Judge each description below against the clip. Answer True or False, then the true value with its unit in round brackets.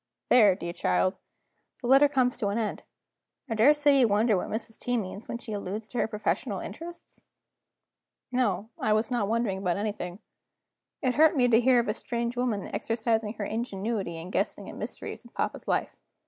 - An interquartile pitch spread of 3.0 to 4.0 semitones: True (3.3 semitones)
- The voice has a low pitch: False (225 Hz)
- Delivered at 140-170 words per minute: False (185 wpm)